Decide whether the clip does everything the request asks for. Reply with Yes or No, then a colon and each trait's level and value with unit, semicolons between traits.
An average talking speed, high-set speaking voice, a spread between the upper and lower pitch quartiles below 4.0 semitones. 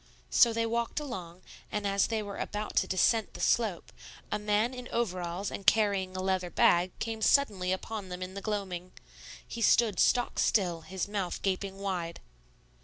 Yes: average, 175 wpm; high, 200 Hz; average, 3.2 semitones